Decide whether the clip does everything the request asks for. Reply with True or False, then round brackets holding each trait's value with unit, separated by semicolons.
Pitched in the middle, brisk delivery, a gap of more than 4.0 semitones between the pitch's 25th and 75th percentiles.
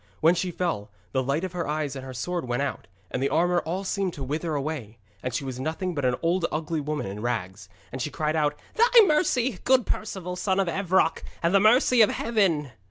True (160 Hz; 225 wpm; 5.6 semitones)